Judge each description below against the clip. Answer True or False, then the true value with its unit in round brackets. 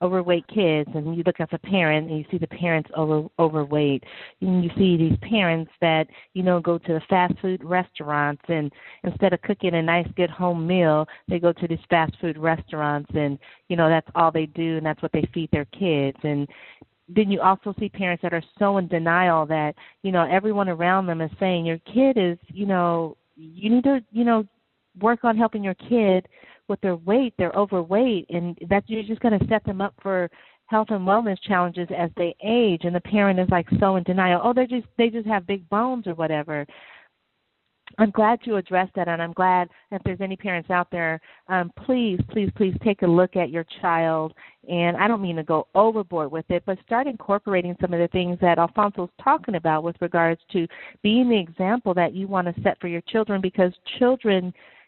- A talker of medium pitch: True (180 Hz)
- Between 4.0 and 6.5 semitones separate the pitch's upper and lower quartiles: False (3.3 semitones)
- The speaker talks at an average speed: False (210 wpm)